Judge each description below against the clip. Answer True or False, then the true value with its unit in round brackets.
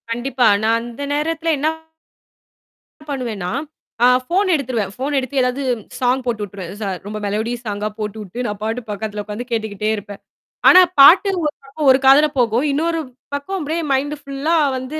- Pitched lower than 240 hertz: False (250 Hz)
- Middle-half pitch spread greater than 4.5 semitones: True (4.9 semitones)